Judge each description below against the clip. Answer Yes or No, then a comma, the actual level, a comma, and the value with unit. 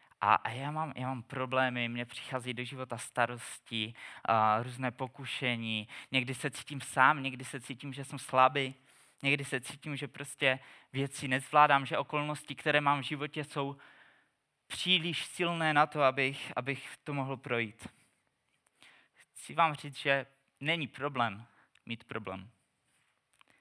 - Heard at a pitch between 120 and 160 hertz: Yes, low, 135 Hz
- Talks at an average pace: Yes, average, 140 wpm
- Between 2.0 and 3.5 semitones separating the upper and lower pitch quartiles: Yes, narrow, 2.6 semitones